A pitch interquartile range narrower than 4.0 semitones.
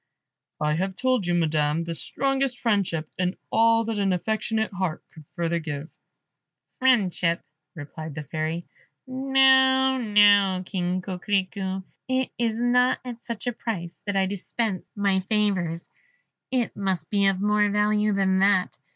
No: average, 4.5 semitones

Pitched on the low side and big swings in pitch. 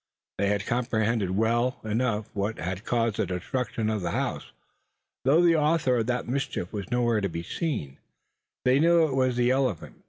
No: low, 115 Hz; average, 3.9 semitones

